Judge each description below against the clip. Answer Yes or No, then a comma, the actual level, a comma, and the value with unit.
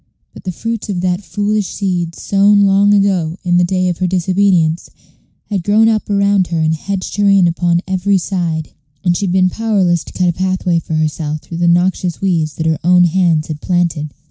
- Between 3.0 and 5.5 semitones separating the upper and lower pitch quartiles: No, narrow, 2.6 semitones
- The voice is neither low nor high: Yes, medium, 180 Hz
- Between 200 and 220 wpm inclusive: Yes, fast, 205 wpm